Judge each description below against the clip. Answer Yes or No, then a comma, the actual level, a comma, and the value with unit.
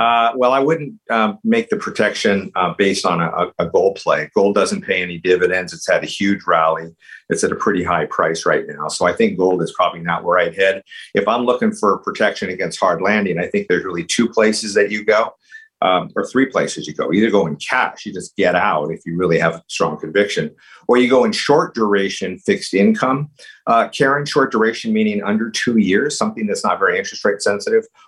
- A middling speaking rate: No, fast, 220 wpm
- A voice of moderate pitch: No, low, 130 Hz